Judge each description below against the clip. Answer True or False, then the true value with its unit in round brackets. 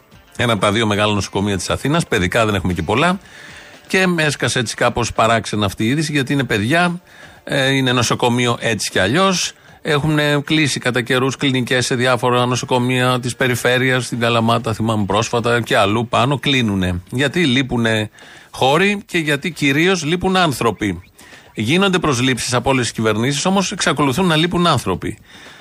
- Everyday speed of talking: True (155 wpm)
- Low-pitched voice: True (125 Hz)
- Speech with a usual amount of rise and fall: True (4.6 semitones)